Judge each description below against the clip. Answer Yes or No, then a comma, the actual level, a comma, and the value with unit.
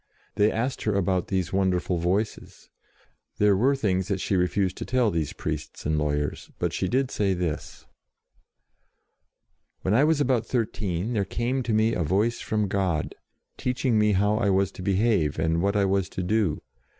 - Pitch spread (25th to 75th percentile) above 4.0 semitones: No, average, 3.6 semitones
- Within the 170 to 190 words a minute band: Yes, average, 180 wpm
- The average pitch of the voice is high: No, low, 100 Hz